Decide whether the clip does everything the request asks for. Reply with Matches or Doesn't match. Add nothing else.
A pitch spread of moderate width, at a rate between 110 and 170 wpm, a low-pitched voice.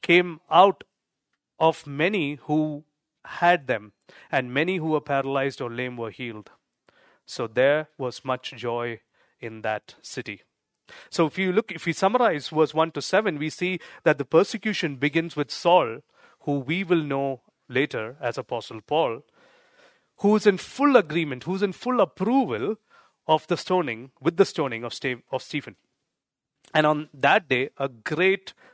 Doesn't match